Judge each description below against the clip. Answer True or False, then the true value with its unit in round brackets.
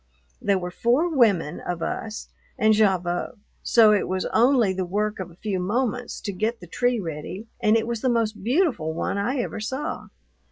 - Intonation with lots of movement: False (4.2 semitones)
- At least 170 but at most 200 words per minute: True (190 wpm)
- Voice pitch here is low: False (215 Hz)